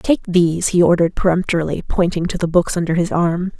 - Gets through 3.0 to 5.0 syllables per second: No, 6.1 syllables/s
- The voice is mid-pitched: Yes, medium, 175 Hz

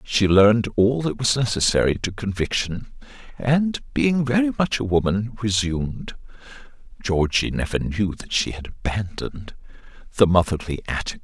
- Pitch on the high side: No, low, 105 Hz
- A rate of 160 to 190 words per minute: No, slow, 135 wpm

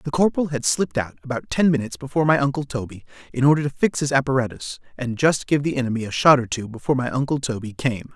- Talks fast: Yes, fast, 235 wpm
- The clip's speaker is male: Yes, male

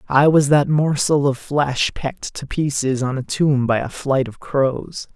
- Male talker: Yes, male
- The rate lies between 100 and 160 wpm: No, average, 200 wpm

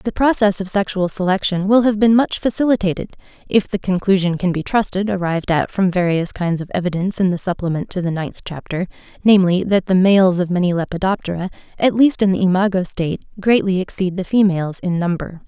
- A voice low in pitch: No, high, 190 Hz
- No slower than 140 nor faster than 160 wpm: No, average, 190 wpm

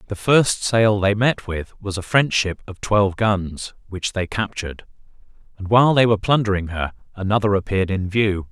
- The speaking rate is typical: Yes, average, 185 wpm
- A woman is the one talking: No, male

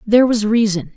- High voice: Yes, high, 215 Hz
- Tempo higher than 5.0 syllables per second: Yes, 6.0 syllables/s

